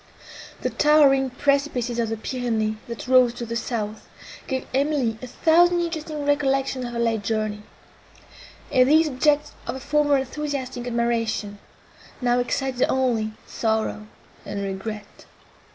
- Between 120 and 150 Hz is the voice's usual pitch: No, very high, 250 Hz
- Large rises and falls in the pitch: No, average, 4.0 semitones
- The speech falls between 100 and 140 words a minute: Yes, slow, 135 wpm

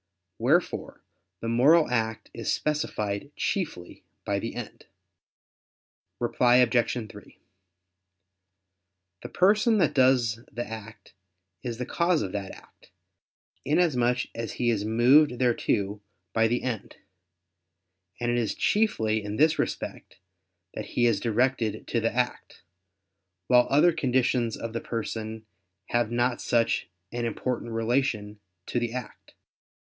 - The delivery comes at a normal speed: No, slow, 125 wpm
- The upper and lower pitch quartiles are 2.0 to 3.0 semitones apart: Yes, narrow, 2.5 semitones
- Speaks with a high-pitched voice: No, low, 120 Hz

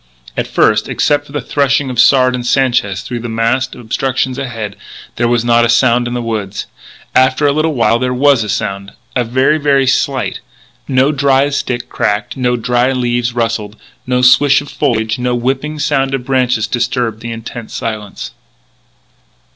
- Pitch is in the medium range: No, low, 125 Hz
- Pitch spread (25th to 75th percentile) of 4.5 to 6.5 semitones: No, narrow, 2.6 semitones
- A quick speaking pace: No, average, 170 wpm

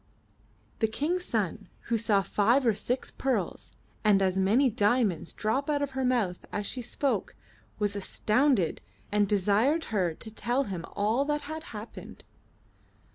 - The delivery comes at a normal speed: Yes, average, 150 wpm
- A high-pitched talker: Yes, high, 220 Hz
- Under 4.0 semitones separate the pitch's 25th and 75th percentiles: No, average, 4.6 semitones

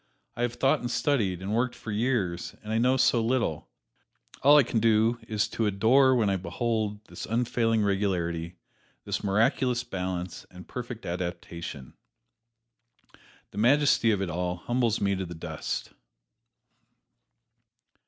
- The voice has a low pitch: Yes, low, 110 Hz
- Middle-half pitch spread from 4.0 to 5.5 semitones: Yes, average, 4.5 semitones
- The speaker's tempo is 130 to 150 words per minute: Yes, average, 145 wpm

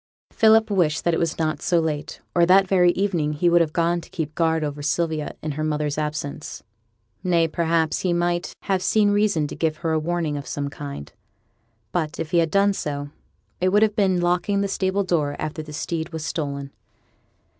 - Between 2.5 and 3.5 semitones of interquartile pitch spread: Yes, average, 3.0 semitones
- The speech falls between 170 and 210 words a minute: Yes, average, 200 wpm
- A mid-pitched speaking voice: Yes, medium, 165 Hz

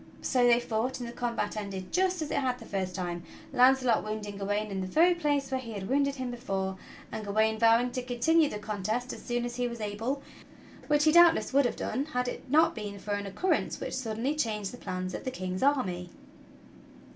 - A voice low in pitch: No, high, 240 Hz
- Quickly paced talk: Yes, fast, 220 wpm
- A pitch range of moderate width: Yes, average, 4.6 semitones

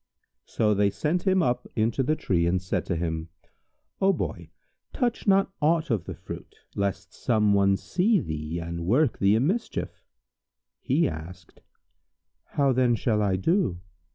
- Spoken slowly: No, average, 155 wpm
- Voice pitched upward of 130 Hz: No, low, 110 Hz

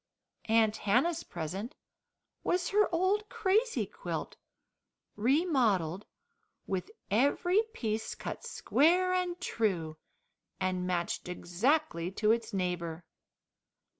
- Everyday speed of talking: No, slow, 95 wpm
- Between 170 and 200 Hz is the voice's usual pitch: No, high, 225 Hz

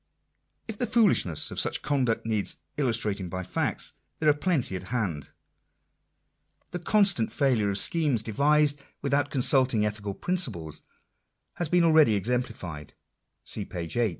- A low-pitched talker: Yes, low, 125 Hz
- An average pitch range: No, wide, 6.8 semitones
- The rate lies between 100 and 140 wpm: Yes, slow, 135 wpm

